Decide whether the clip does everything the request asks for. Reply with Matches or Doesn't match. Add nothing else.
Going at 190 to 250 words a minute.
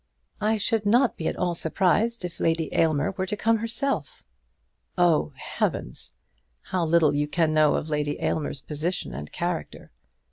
Doesn't match